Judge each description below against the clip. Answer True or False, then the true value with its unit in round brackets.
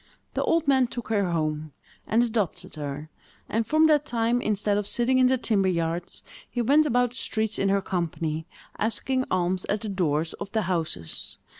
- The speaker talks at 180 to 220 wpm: True (185 wpm)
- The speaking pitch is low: False (205 Hz)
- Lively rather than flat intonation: True (6.0 semitones)